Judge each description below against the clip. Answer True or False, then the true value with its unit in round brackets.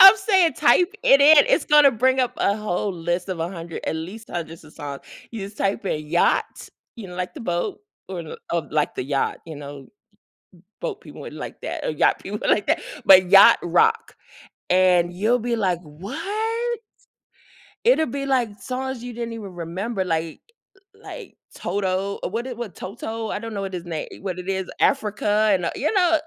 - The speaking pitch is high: True (200 Hz)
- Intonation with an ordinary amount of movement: False (6.7 semitones)